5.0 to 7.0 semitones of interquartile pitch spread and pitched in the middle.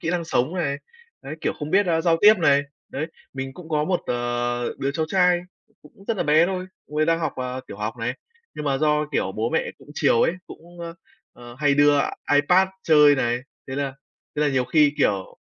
No: average, 3.9 semitones; medium, 150 Hz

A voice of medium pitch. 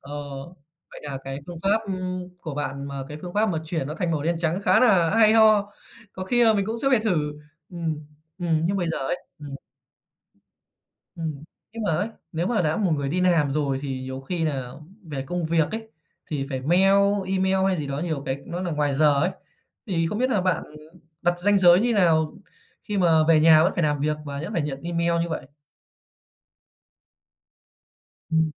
Yes: medium, 165 Hz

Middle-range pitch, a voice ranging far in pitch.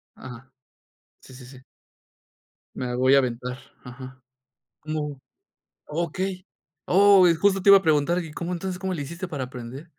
Yes: medium, 150 Hz; wide, 5.8 semitones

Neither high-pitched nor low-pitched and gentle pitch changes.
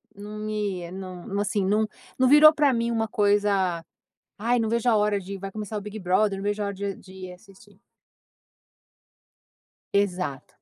No: high, 205 Hz; narrow, 2.0 semitones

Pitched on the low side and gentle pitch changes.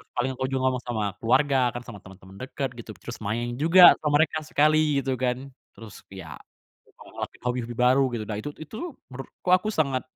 No: low, 130 Hz; average, 4.2 semitones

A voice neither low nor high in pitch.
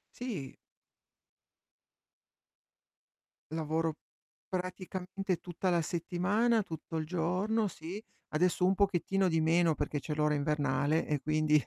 Yes: medium, 170 Hz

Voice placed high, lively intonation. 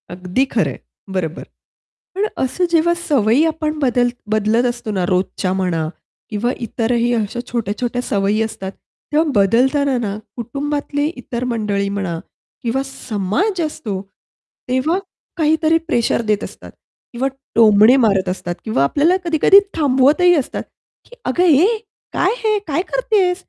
Yes: high, 245 Hz; wide, 6.7 semitones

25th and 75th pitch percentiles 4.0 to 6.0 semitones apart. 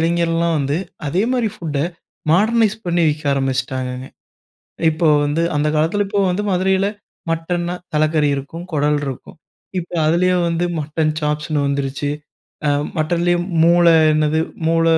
No: average, 2.9 semitones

